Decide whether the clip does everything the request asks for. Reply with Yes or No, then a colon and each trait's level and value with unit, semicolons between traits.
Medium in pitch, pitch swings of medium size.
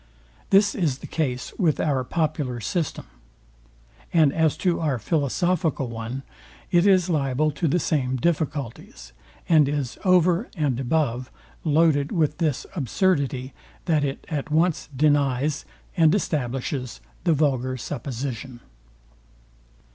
Yes: medium, 150 Hz; average, 3.9 semitones